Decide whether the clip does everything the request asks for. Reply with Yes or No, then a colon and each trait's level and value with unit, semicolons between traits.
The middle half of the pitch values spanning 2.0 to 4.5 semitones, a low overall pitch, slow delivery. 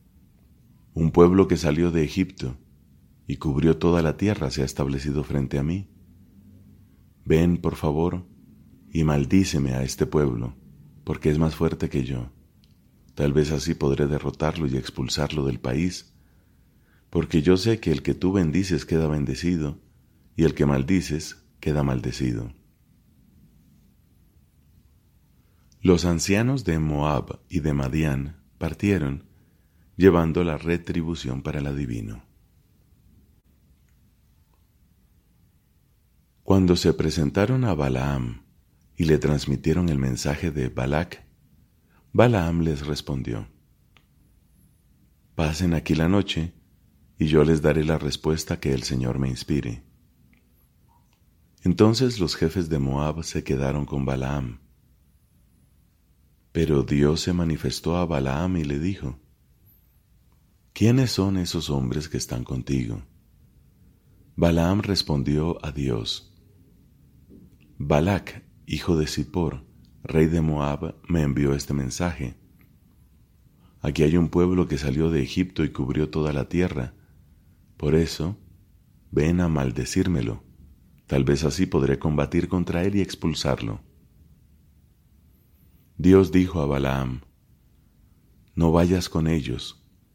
Yes: average, 3.8 semitones; very low, 80 Hz; slow, 115 wpm